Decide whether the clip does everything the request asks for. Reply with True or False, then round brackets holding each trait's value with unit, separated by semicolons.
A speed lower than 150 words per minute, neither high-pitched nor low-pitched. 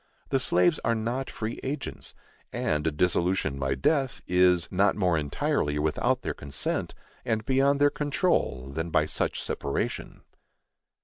False (140 wpm; 90 Hz)